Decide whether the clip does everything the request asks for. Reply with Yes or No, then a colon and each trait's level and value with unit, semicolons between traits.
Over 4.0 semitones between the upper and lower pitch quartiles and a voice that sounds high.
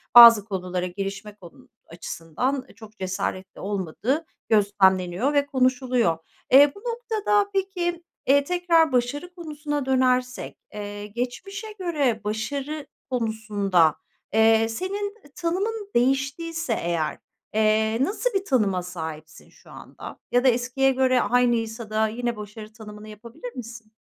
Yes: wide, 5.6 semitones; high, 240 Hz